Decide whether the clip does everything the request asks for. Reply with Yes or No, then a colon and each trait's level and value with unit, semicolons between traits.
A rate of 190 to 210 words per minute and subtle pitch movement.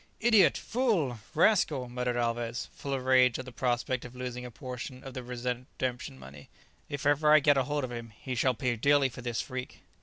Yes: average, 200 wpm; narrow, 2.3 semitones